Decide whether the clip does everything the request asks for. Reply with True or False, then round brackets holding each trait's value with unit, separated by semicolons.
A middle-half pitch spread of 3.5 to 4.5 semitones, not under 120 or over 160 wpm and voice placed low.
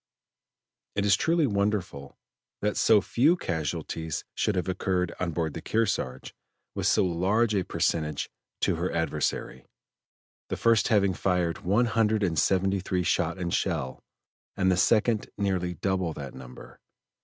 True (3.8 semitones; 145 wpm; 95 Hz)